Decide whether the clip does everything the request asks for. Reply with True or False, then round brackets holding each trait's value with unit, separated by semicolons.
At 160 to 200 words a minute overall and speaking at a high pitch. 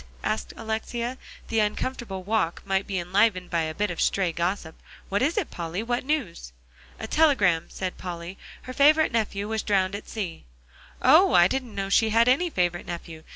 True (180 wpm; 200 Hz)